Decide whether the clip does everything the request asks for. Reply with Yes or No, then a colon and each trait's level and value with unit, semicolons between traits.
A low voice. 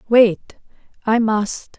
No: high, 220 Hz